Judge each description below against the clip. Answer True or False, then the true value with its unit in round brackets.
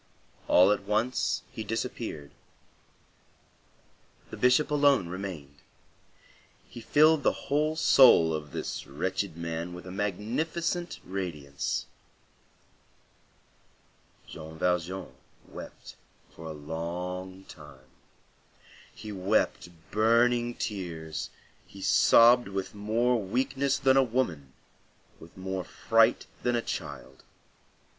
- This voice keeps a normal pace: False (100 wpm)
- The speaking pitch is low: True (95 Hz)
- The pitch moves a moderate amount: False (6.3 semitones)